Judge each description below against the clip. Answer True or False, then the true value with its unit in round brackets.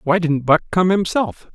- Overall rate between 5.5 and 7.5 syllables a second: False (4.6 syllables/s)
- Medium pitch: True (170 Hz)